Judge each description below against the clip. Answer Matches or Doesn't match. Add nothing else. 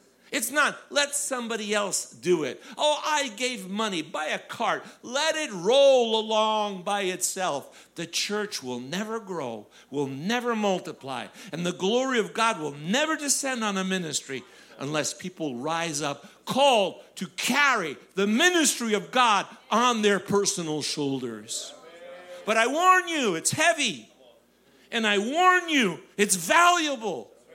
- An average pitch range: Doesn't match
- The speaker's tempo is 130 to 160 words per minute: Matches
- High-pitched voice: Matches